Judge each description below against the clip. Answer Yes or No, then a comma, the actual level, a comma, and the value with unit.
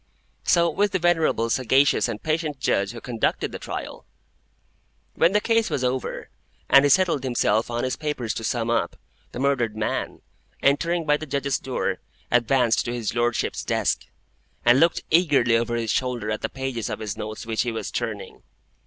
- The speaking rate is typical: Yes, average, 180 wpm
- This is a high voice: No, low, 125 Hz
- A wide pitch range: No, average, 4.3 semitones